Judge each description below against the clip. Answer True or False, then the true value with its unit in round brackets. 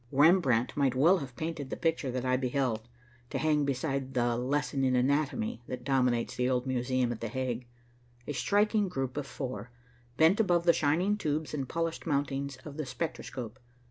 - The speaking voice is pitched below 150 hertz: True (135 Hz)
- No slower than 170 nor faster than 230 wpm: True (175 wpm)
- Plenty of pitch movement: False (3.7 semitones)